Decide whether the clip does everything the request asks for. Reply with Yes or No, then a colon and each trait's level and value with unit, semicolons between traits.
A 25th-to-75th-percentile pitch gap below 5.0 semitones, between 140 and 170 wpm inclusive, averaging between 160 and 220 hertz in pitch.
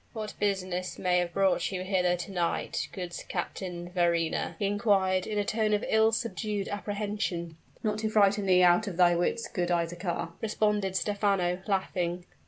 Yes: average, 2.8 semitones; average, 165 wpm; high, 190 Hz